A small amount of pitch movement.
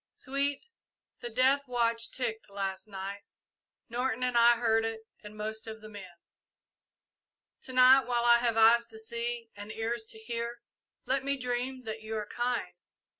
Yes: narrow, 2.0 semitones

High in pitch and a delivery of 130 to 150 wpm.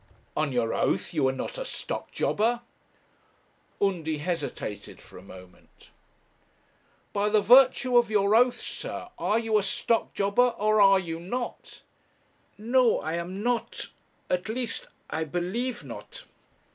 Yes: high, 205 Hz; average, 140 wpm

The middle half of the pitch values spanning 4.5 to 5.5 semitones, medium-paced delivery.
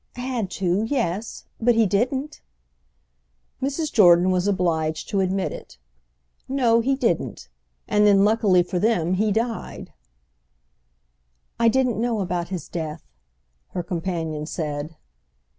No: average, 4.9 semitones; slow, 120 wpm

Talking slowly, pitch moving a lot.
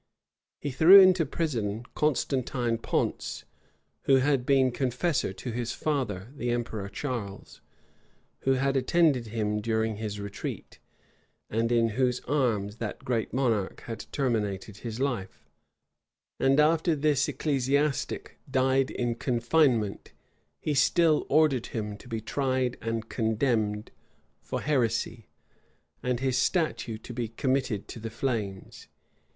No: slow, 125 wpm; average, 3.7 semitones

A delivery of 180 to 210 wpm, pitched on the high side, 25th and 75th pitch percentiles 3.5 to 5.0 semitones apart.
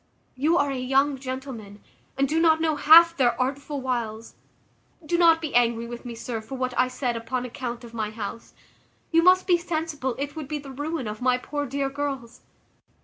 Yes: average, 200 wpm; very high, 265 Hz; average, 3.8 semitones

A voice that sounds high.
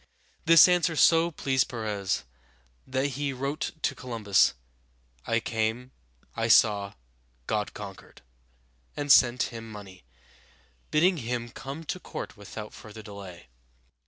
No: low, 120 Hz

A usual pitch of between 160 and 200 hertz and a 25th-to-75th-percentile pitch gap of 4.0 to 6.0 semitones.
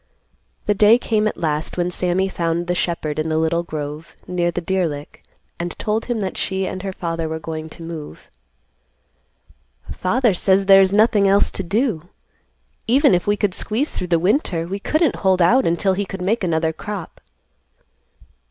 No: medium, 185 Hz; average, 3.5 semitones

